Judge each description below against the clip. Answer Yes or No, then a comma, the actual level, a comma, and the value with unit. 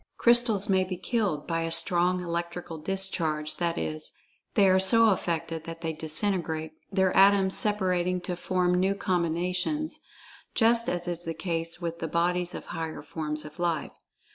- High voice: No, medium, 175 Hz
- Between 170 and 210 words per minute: No, average, 155 wpm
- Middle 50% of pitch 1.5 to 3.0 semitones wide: Yes, narrow, 2.5 semitones